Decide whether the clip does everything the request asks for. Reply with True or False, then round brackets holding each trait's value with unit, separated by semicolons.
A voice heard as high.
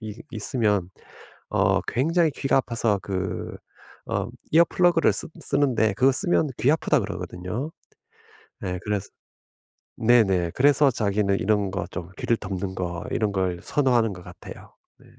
False (110 Hz)